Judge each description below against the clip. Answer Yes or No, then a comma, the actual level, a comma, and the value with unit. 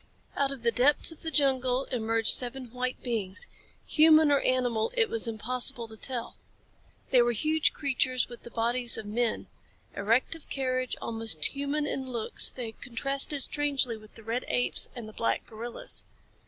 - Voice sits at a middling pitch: No, very high, 250 Hz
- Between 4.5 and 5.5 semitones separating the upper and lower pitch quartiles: No, average, 3.3 semitones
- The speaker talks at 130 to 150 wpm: No, average, 170 wpm